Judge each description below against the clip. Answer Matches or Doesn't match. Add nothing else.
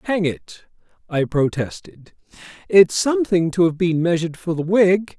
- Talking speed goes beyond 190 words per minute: Doesn't match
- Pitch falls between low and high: Matches